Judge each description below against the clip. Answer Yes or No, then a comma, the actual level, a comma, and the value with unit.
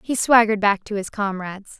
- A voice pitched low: No, high, 210 Hz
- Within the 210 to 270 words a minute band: No, average, 200 wpm